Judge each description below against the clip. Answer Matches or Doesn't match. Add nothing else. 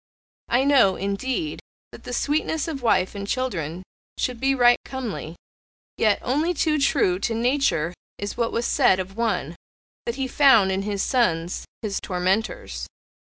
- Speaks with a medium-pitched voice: Doesn't match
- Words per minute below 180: Matches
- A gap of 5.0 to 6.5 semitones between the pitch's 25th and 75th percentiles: Matches